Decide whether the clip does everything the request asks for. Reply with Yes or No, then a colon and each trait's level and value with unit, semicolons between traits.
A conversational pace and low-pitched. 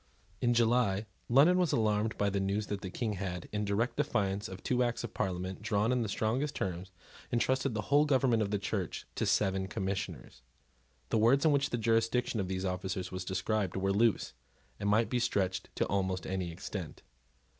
Yes: average, 190 wpm; low, 105 Hz